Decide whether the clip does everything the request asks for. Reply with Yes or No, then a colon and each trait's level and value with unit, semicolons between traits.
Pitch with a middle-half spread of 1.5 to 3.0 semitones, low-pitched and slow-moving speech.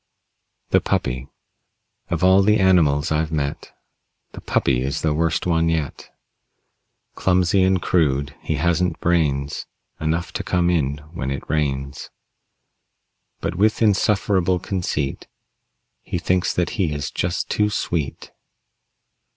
No: average, 4.1 semitones; very low, 80 Hz; slow, 125 wpm